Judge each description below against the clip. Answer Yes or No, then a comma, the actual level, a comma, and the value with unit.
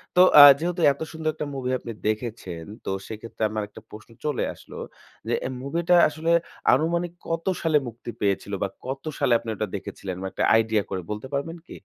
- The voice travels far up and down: Yes, wide, 6.9 semitones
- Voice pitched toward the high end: No, low, 125 Hz